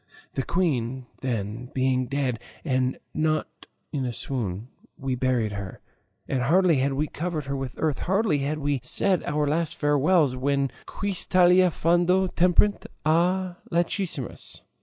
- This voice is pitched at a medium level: Yes, medium, 145 Hz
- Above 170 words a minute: No, average, 140 wpm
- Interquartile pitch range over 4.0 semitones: Yes, average, 5.2 semitones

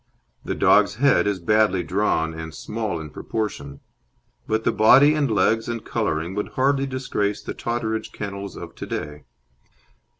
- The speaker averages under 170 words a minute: Yes, average, 155 wpm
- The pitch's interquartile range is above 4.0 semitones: Yes, average, 4.7 semitones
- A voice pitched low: Yes, low, 105 Hz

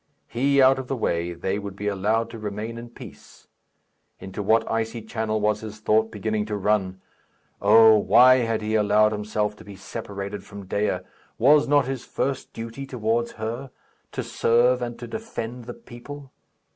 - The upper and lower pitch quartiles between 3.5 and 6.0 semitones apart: No, narrow, 2.6 semitones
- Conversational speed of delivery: Yes, average, 170 wpm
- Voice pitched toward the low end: Yes, low, 110 Hz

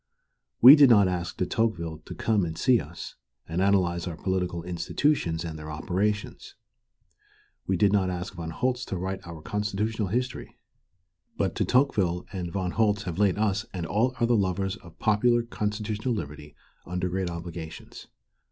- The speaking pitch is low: Yes, very low, 95 Hz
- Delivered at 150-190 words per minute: Yes, average, 160 wpm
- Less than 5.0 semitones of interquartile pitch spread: Yes, average, 3.7 semitones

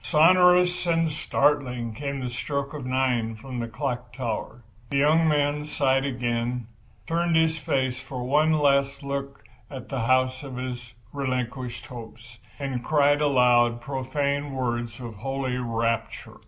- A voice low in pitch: Yes, low, 130 Hz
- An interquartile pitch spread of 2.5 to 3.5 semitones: Yes, average, 2.9 semitones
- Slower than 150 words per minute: Yes, average, 140 wpm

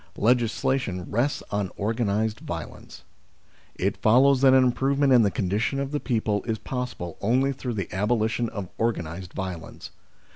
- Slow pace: No, average, 150 wpm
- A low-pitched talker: Yes, low, 115 Hz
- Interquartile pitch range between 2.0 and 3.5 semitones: No, average, 4.2 semitones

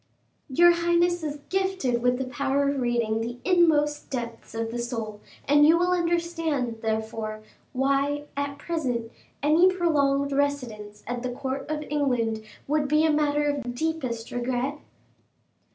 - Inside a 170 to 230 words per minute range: No, average, 150 wpm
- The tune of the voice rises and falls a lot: No, average, 4.3 semitones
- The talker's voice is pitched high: Yes, very high, 280 Hz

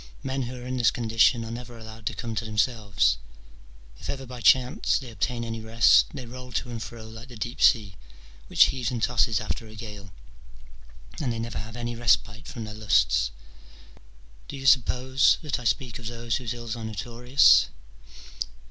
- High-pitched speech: No, low, 115 Hz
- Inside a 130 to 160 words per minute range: No, average, 185 wpm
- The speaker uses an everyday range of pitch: No, narrow, 2.1 semitones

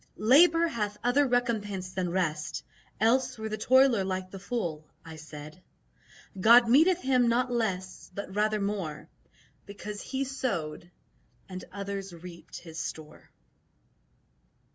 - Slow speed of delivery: Yes, slow, 125 wpm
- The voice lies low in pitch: No, high, 205 Hz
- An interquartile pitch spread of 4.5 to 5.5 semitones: Yes, average, 5.1 semitones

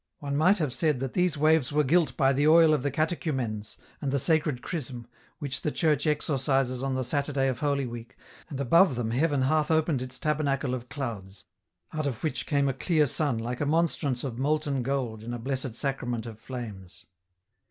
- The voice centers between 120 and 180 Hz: Yes, medium, 140 Hz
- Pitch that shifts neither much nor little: Yes, average, 3.5 semitones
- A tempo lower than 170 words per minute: No, average, 195 wpm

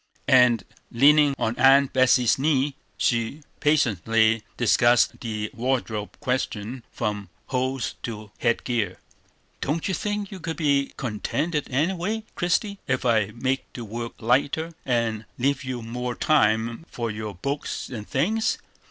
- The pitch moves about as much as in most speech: Yes, average, 4.2 semitones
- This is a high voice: No, low, 125 Hz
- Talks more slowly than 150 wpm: Yes, slow, 135 wpm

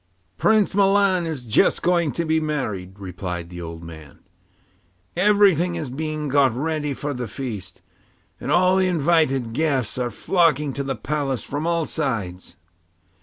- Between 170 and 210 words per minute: No, average, 150 wpm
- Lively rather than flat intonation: Yes, wide, 6.7 semitones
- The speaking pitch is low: No, medium, 145 Hz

